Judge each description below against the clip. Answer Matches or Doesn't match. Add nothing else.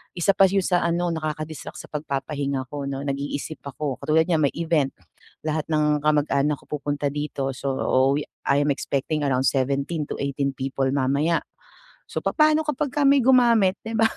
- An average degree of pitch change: Matches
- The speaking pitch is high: Doesn't match